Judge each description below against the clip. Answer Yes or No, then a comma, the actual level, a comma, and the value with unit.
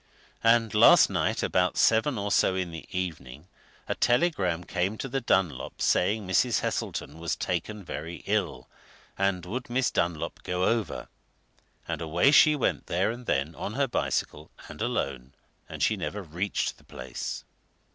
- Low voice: Yes, very low, 95 Hz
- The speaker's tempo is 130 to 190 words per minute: Yes, average, 155 wpm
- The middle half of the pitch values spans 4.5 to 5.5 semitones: Yes, average, 5.2 semitones